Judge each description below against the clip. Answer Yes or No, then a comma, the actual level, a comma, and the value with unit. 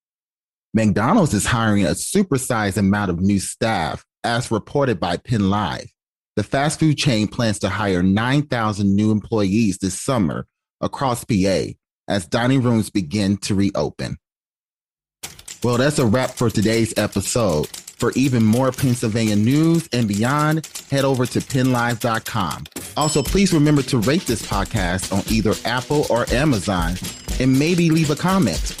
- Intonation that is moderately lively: Yes, average, 4.9 semitones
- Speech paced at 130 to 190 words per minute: Yes, average, 140 wpm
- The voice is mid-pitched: No, low, 115 Hz